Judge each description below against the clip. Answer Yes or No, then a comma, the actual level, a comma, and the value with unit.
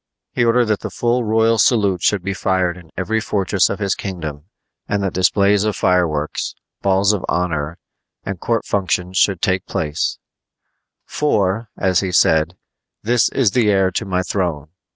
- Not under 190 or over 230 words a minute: No, average, 165 wpm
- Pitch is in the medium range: No, very low, 95 Hz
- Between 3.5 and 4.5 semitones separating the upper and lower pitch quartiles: No, average, 2.8 semitones